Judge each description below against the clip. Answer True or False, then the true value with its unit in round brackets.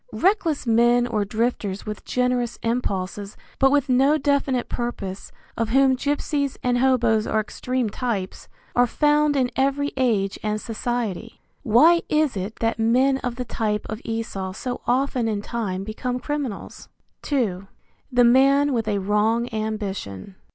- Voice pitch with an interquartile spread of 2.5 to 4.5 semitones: True (3.7 semitones)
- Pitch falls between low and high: False (240 Hz)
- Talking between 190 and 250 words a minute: False (145 wpm)